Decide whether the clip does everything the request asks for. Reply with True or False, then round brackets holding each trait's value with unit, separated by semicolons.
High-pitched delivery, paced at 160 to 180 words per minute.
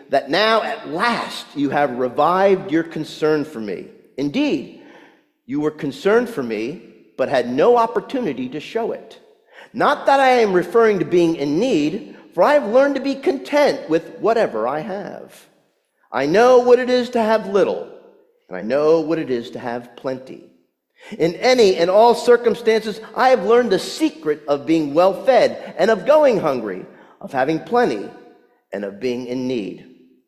True (215 Hz; 170 wpm)